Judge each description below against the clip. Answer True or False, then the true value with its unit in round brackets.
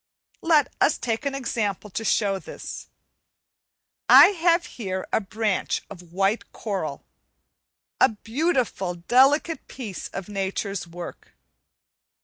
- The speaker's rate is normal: False (115 wpm)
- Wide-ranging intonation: True (5.8 semitones)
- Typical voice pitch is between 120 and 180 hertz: False (215 Hz)